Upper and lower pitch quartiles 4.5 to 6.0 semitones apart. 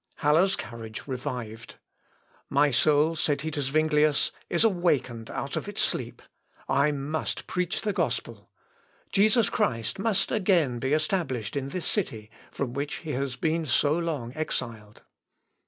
Yes: average, 4.9 semitones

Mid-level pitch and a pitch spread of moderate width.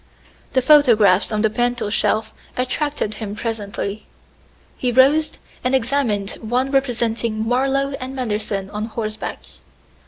No: high, 235 Hz; average, 3.5 semitones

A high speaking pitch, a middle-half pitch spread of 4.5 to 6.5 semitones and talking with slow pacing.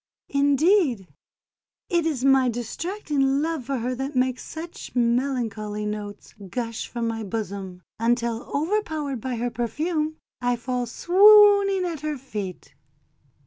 Yes: very high, 255 Hz; average, 5.2 semitones; slow, 125 wpm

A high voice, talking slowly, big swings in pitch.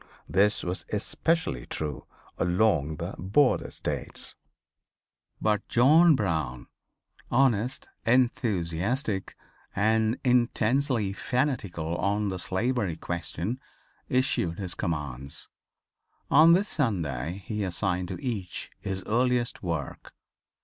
No: low, 100 Hz; slow, 95 wpm; wide, 6.3 semitones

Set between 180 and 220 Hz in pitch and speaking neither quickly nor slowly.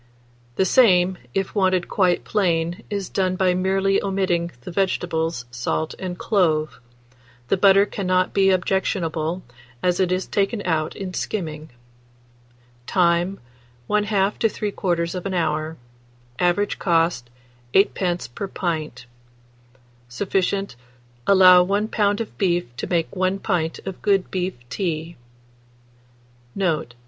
No: medium, 185 Hz; slow, 115 wpm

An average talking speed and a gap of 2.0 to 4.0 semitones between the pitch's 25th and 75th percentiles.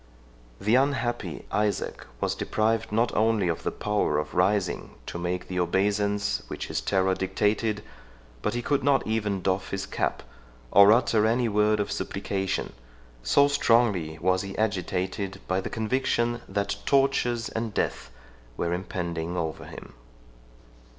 Yes: average, 145 wpm; average, 3.3 semitones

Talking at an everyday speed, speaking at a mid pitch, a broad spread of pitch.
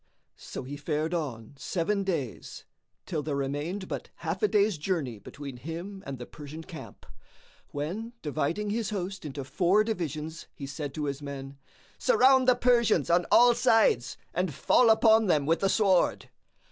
Yes: average, 160 wpm; medium, 165 Hz; wide, 6.4 semitones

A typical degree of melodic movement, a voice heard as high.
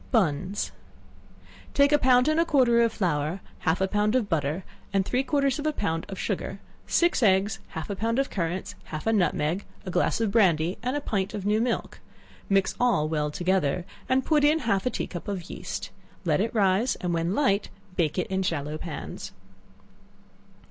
No: wide, 6.0 semitones; high, 195 Hz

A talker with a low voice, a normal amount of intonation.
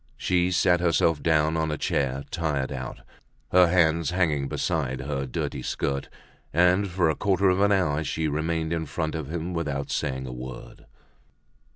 Yes: very low, 80 Hz; average, 3.6 semitones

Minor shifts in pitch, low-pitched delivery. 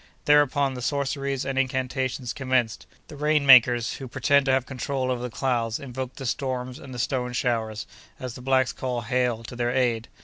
Yes: narrow, 1.7 semitones; low, 130 Hz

